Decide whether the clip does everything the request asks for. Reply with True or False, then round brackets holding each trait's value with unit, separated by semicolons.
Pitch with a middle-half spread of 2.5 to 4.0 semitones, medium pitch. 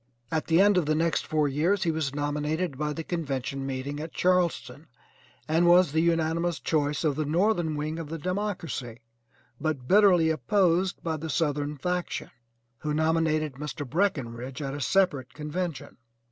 True (3.0 semitones; 155 Hz)